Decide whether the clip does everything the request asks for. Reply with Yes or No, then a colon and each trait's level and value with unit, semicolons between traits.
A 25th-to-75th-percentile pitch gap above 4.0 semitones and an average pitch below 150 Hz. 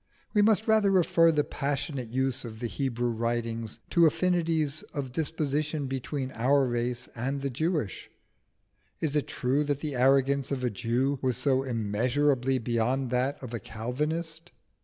No: average, 3.5 semitones; low, 135 Hz